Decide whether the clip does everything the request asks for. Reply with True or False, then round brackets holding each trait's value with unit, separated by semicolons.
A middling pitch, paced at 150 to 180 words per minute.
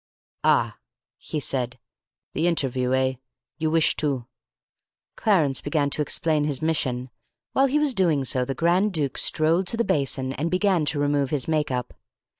True (150 Hz; 170 wpm)